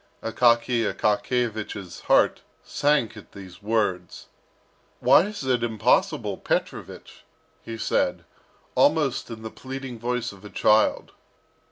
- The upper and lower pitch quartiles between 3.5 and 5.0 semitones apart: No, average, 2.8 semitones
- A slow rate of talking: Yes, slow, 115 wpm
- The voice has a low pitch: Yes, low, 115 Hz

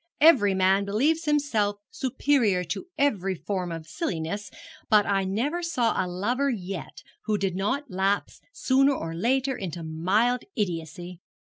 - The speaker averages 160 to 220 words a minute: No, average, 140 wpm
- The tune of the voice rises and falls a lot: Yes, wide, 6.5 semitones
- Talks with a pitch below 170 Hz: No, high, 205 Hz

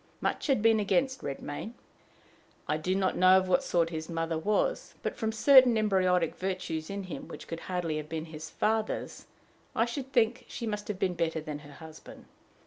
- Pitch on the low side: No, medium, 185 Hz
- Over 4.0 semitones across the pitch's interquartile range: Yes, average, 5.3 semitones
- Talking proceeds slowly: No, average, 190 wpm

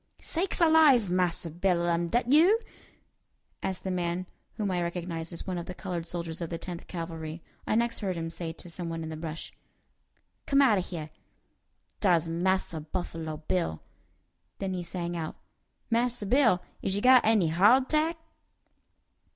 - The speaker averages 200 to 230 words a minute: No, average, 165 wpm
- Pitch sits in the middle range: Yes, medium, 180 Hz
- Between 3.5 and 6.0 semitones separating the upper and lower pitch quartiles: Yes, average, 4.4 semitones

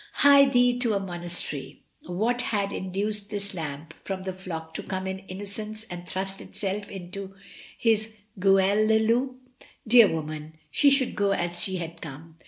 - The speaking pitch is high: Yes, high, 195 Hz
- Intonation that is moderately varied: Yes, average, 3.6 semitones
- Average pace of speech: Yes, average, 165 wpm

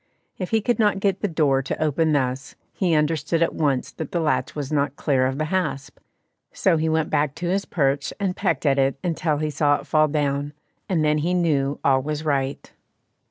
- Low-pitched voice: No, medium, 150 Hz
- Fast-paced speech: Yes, fast, 210 wpm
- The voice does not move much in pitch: No, average, 3.0 semitones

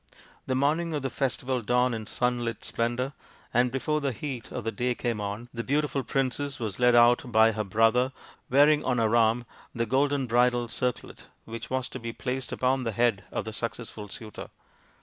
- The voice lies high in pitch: No, low, 120 Hz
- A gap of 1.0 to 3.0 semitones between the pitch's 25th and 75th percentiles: Yes, narrow, 2.4 semitones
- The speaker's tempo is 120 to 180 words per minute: No, average, 190 wpm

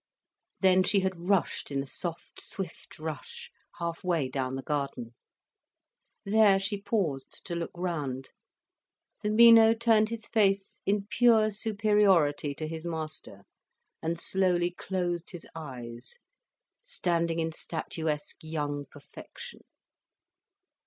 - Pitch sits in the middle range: Yes, medium, 175 Hz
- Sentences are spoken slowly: Yes, slow, 120 wpm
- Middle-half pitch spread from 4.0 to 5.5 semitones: Yes, average, 4.8 semitones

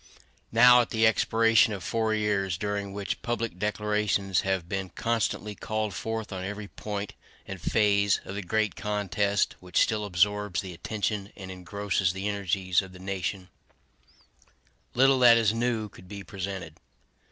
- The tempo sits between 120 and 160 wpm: Yes, average, 150 wpm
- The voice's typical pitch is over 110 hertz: No, low, 100 Hz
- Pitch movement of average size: No, narrow, 2.2 semitones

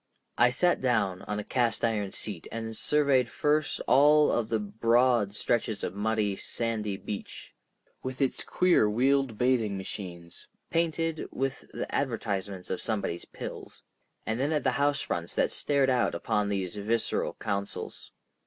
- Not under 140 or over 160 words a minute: Yes, average, 145 wpm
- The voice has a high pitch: No, low, 115 Hz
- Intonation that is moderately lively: Yes, average, 4.5 semitones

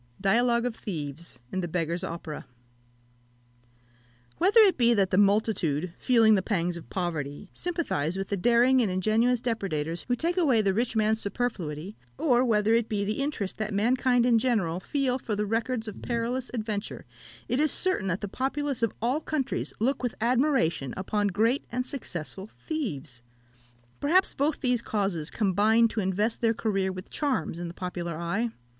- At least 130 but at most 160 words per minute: No, average, 170 wpm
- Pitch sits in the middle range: No, high, 220 Hz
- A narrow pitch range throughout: No, average, 5.0 semitones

